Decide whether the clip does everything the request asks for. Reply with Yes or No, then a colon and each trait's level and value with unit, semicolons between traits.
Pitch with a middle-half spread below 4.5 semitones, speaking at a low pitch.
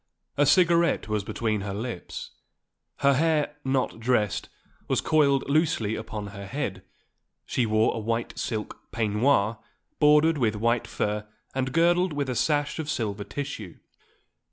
No: wide, 5.5 semitones; low, 125 Hz